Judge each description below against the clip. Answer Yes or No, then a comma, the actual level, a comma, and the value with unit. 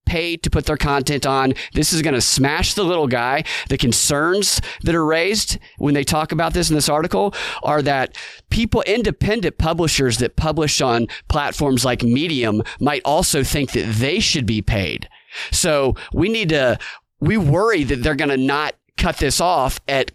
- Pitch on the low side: No, medium, 145 Hz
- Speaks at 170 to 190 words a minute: Yes, average, 180 wpm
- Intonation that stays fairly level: No, average, 3.5 semitones